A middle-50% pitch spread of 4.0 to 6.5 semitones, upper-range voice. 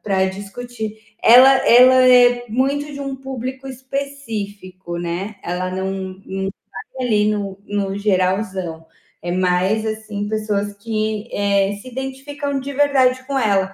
Yes: average, 5.0 semitones; high, 215 Hz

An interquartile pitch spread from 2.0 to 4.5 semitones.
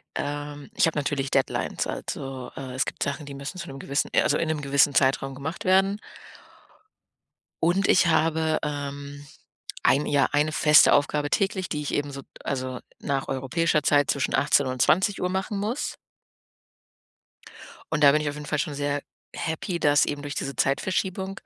Yes: average, 2.7 semitones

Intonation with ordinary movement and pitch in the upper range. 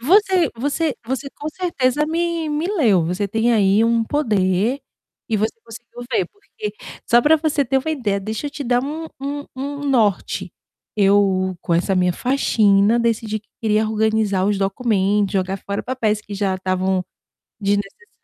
No: wide, 6.0 semitones; high, 225 Hz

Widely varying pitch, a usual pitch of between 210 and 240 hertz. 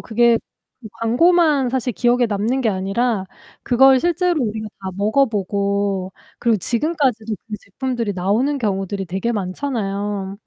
No: average, 4.3 semitones; high, 220 Hz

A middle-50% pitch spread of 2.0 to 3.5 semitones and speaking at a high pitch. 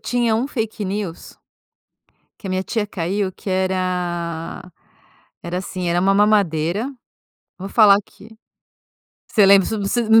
Yes: average, 2.8 semitones; high, 195 Hz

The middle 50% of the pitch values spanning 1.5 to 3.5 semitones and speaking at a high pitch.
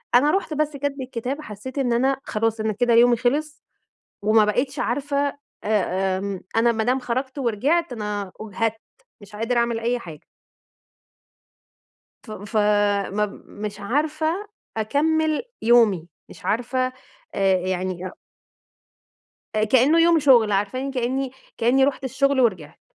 No: average, 4.5 semitones; high, 240 Hz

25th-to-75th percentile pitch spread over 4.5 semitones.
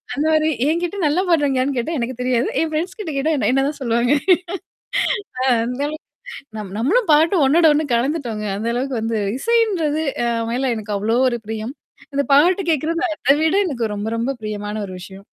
Yes: average, 5.2 semitones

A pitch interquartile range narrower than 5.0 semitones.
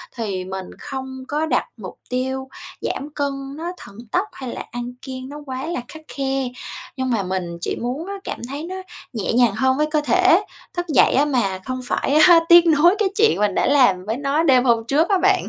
Yes: average, 4.2 semitones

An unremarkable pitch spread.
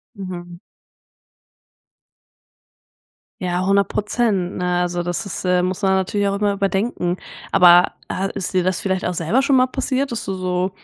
No: narrow, 2.1 semitones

